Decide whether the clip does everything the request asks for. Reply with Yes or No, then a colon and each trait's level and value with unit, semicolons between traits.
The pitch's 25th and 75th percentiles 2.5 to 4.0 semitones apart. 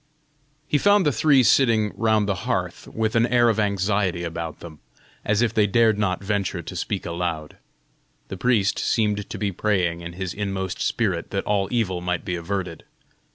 Yes: average, 3.6 semitones